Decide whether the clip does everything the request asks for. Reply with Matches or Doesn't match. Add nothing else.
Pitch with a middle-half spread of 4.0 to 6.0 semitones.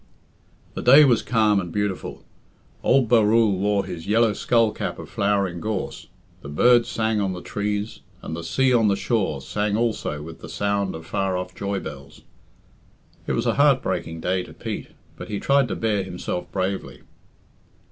Doesn't match